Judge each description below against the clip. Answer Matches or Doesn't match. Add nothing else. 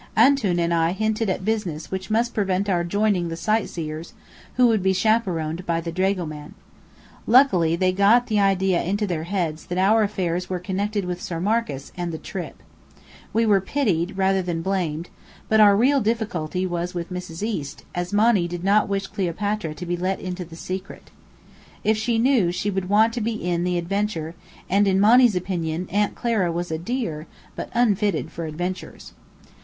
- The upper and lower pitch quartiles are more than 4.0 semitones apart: Doesn't match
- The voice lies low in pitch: Doesn't match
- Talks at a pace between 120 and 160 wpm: Doesn't match